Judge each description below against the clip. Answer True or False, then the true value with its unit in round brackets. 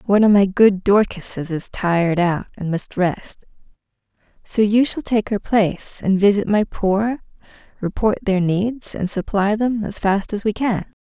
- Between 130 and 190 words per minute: True (175 wpm)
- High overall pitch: True (200 Hz)